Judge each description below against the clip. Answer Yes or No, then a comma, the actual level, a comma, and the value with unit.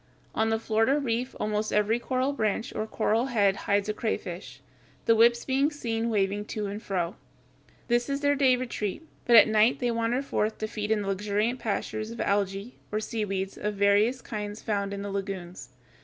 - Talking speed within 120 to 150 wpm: No, average, 185 wpm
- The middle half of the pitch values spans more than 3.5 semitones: No, average, 2.8 semitones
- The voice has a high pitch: Yes, high, 215 Hz